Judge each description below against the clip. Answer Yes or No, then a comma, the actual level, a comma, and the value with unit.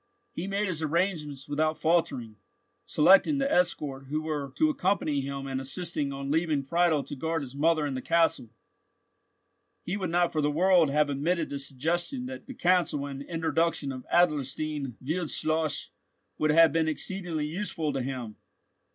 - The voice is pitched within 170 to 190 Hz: No, medium, 155 Hz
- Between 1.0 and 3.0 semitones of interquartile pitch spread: No, average, 3.7 semitones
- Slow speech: No, average, 160 wpm